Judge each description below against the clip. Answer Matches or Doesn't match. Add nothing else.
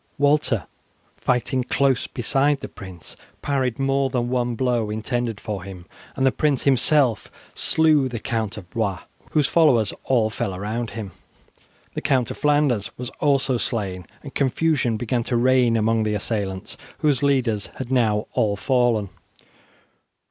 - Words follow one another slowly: Doesn't match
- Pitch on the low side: Matches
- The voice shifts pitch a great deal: Doesn't match